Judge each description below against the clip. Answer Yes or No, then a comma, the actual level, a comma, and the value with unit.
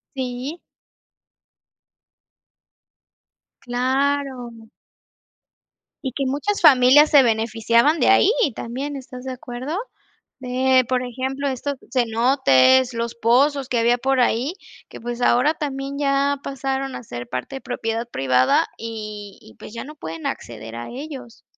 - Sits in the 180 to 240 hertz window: No, very high, 255 Hz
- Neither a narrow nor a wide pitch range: Yes, average, 3.0 semitones